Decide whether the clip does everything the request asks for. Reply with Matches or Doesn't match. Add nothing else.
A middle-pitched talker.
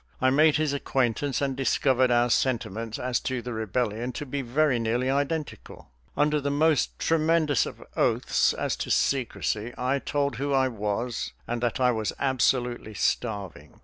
Doesn't match